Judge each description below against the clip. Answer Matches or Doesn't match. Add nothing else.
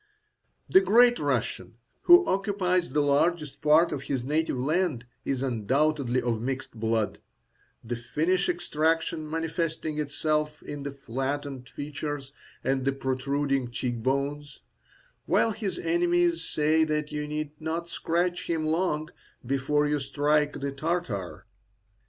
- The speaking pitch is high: Doesn't match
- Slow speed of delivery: Matches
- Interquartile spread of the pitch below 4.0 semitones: Matches